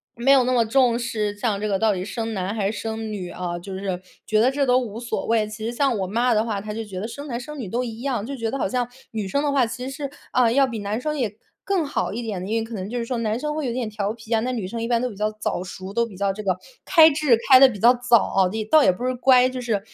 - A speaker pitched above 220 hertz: Yes, high, 230 Hz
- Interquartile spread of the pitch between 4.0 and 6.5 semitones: No, average, 3.3 semitones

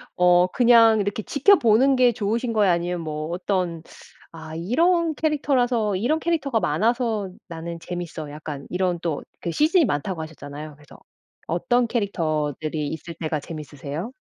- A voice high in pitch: No, medium, 180 Hz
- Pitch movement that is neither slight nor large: No, wide, 7.0 semitones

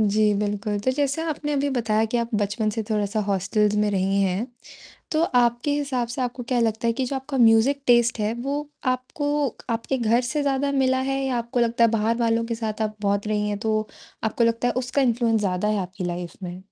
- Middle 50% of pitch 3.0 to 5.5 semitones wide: Yes, average, 3.6 semitones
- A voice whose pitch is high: Yes, high, 230 Hz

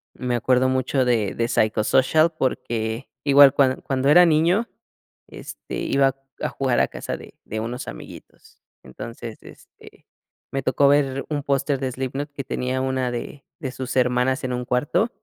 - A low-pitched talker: Yes, low, 130 Hz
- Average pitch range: No, narrow, 2.1 semitones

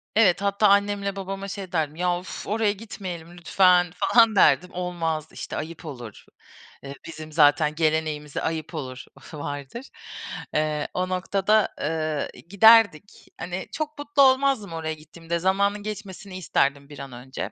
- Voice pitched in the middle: Yes, medium, 180 Hz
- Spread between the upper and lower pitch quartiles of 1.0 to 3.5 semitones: No, average, 4.5 semitones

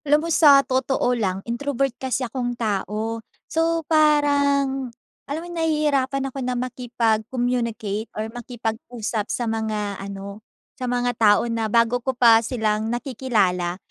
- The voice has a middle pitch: No, high, 245 Hz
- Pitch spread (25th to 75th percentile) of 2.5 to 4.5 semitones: Yes, average, 3.5 semitones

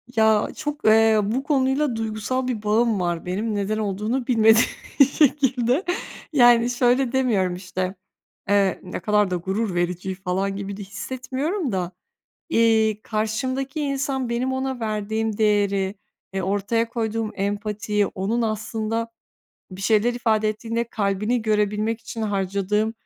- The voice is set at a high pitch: Yes, high, 220 Hz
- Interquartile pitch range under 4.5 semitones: Yes, average, 3.1 semitones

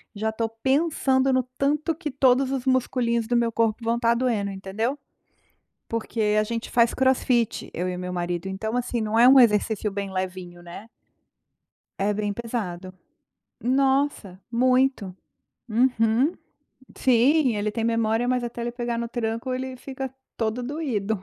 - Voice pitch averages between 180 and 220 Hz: No, high, 235 Hz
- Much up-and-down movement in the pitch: No, average, 3.5 semitones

